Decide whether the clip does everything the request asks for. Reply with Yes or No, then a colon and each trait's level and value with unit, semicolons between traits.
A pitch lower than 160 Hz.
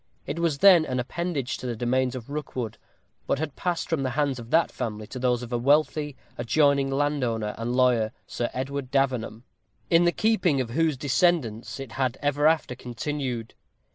Yes: low, 135 Hz